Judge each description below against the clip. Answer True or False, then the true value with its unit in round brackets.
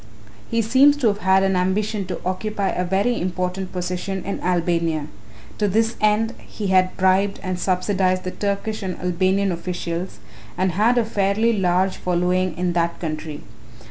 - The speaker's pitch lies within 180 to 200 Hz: True (185 Hz)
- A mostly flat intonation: True (2.2 semitones)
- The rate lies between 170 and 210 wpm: False (160 wpm)